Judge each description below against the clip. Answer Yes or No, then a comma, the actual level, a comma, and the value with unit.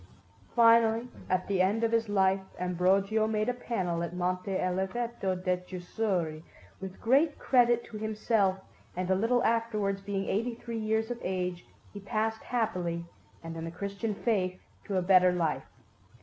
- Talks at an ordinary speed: Yes, average, 160 wpm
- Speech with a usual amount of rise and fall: Yes, average, 3.7 semitones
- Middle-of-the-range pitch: No, high, 200 Hz